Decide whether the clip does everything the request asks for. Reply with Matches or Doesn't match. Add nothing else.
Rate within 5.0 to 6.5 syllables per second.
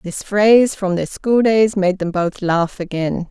Doesn't match